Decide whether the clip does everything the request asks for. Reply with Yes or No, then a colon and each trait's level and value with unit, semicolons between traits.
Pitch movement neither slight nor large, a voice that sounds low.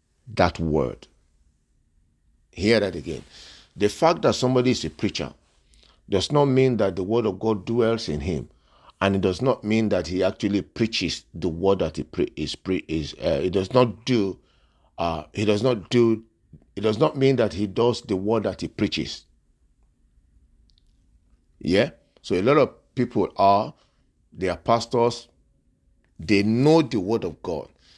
No: wide, 6.4 semitones; very low, 95 Hz